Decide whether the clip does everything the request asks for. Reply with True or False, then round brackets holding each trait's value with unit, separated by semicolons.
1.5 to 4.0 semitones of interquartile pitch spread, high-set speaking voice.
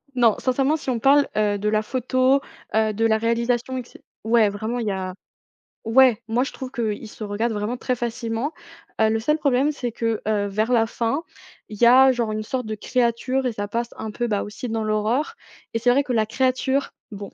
True (2.9 semitones; 235 Hz)